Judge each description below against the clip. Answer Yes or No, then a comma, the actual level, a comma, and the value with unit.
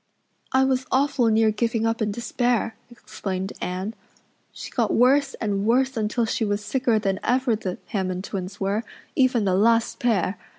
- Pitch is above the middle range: Yes, high, 225 Hz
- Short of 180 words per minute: Yes, average, 165 wpm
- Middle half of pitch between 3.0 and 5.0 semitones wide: Yes, average, 3.3 semitones